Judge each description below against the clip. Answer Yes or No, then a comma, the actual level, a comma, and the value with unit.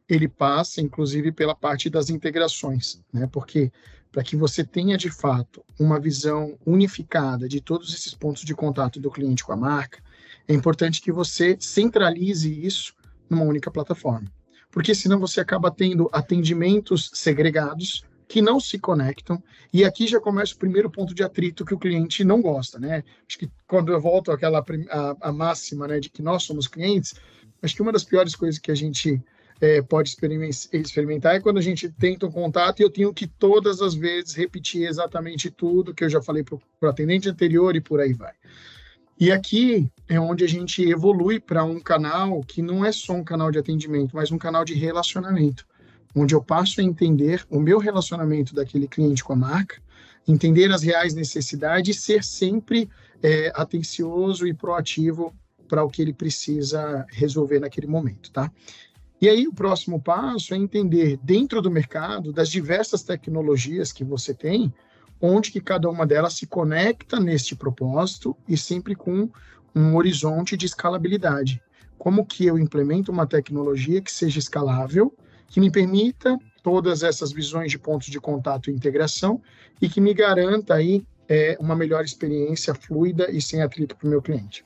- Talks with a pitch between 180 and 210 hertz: No, medium, 165 Hz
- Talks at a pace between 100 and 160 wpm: No, average, 175 wpm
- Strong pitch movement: No, average, 3.6 semitones